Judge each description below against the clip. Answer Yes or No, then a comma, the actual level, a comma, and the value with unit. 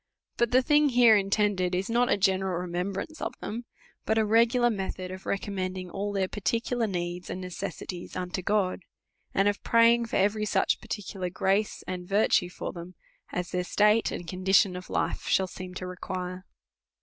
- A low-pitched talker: No, high, 195 Hz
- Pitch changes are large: No, average, 3.0 semitones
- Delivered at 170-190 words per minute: Yes, average, 175 wpm